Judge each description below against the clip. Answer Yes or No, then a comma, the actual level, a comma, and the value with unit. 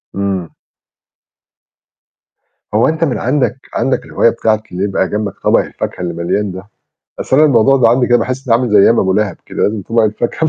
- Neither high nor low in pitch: No, low, 110 Hz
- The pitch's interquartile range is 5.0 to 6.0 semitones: No, average, 4.2 semitones